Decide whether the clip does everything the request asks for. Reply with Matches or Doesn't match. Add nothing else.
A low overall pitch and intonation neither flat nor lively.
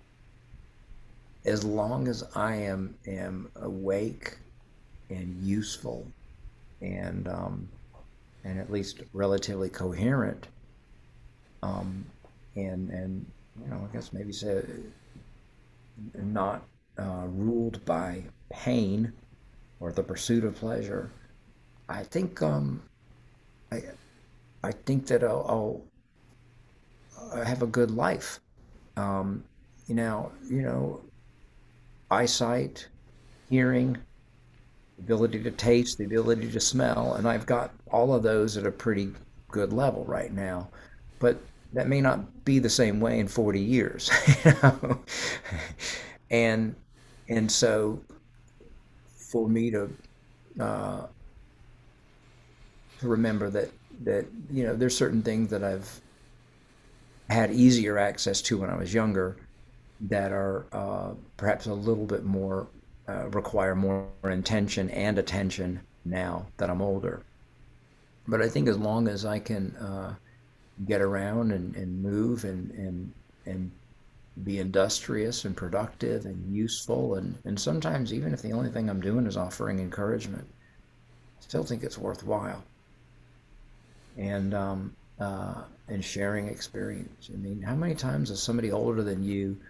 Matches